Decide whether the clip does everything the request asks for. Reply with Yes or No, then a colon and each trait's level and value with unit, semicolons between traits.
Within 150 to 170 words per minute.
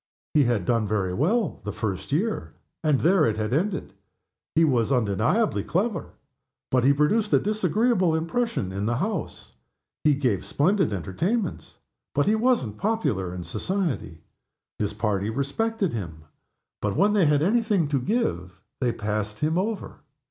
Yes: average, 155 wpm